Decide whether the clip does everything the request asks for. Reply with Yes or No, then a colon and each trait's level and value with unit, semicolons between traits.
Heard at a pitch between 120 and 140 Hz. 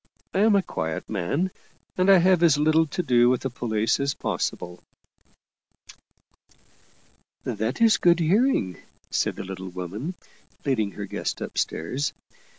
Yes: low, 135 Hz